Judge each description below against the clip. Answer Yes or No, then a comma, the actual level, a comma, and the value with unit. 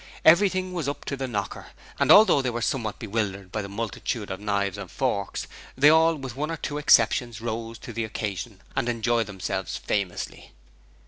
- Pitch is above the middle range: No, low, 115 Hz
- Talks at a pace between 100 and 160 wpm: No, average, 185 wpm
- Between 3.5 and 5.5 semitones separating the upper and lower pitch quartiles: Yes, average, 5.1 semitones